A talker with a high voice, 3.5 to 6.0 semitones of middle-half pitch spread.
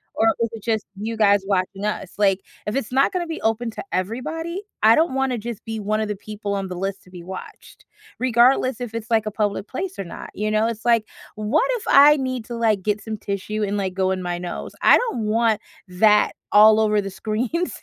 No: high, 215 Hz; average, 3.0 semitones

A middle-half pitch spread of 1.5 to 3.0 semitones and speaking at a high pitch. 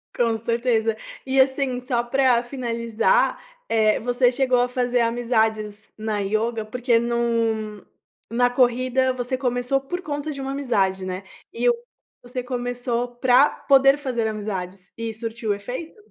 Yes: narrow, 2.6 semitones; high, 240 Hz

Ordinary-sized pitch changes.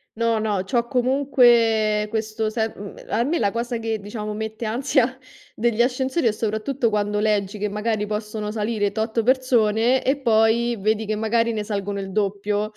No: narrow, 2.0 semitones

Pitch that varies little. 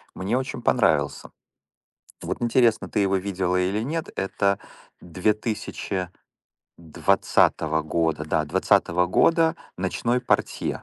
No: average, 4.9 semitones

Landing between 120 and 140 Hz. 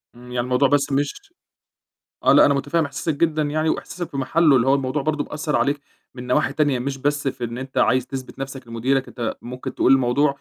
Yes: low, 135 Hz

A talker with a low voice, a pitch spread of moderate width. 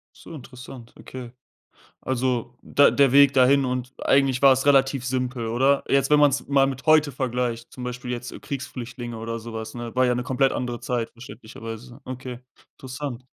No: low, 125 Hz; narrow, 2.0 semitones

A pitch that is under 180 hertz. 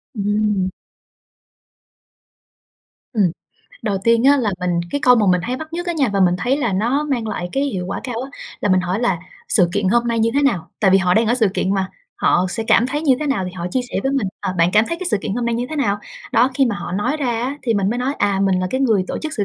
No: high, 225 Hz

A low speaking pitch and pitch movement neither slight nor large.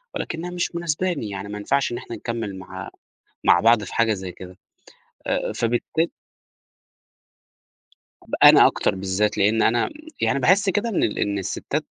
No: low, 115 Hz; wide, 8.4 semitones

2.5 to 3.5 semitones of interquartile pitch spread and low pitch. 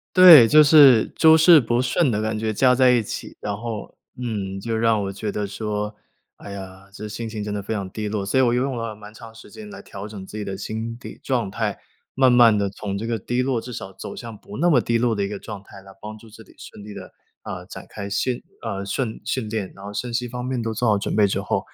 Yes: average, 3.2 semitones; low, 110 Hz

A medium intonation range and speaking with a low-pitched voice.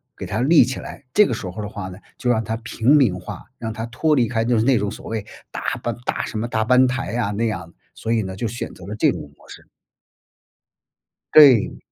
Yes: average, 3.1 semitones; low, 115 Hz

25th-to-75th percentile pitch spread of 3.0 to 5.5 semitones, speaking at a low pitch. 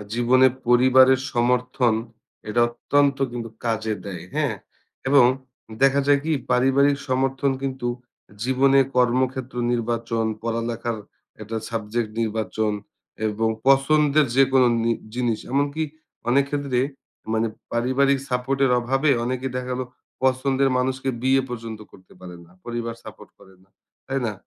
No: narrow, 2.6 semitones; low, 125 Hz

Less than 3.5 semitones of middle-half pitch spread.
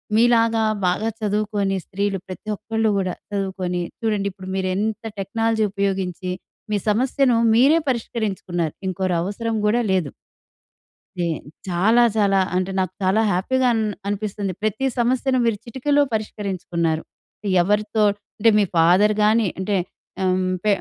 Yes: average, 3.1 semitones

